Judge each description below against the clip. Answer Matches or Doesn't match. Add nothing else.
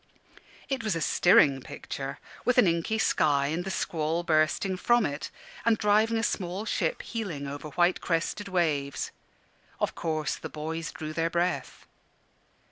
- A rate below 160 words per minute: Matches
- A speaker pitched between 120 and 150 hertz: Doesn't match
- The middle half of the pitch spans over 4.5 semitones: Matches